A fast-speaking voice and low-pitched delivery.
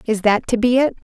No: fast, 270 wpm; high, 230 Hz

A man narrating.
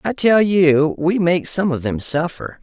No: female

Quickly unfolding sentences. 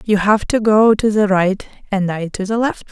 Yes: fast, 245 wpm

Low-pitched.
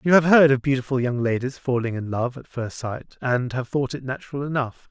Yes: low, 130 Hz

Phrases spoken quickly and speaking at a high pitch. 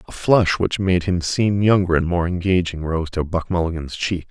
No: fast, 210 wpm; very low, 90 Hz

